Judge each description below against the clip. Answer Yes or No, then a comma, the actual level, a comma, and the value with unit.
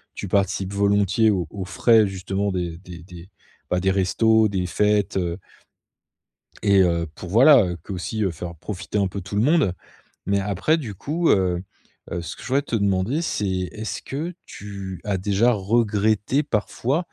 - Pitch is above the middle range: No, low, 100 Hz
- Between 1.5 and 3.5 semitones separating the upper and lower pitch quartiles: Yes, average, 3.0 semitones